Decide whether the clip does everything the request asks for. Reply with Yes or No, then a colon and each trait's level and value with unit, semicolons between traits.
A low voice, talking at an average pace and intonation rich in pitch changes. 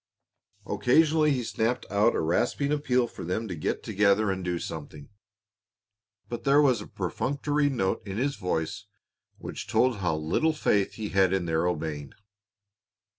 Yes: low, 105 Hz; average, 155 wpm; wide, 6.6 semitones